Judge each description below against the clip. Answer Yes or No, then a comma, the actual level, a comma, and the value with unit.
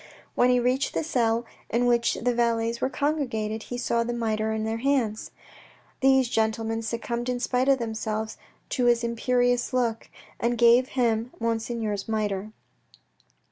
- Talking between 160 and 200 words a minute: No, average, 150 wpm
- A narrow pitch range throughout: Yes, narrow, 1.8 semitones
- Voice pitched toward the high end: Yes, high, 235 Hz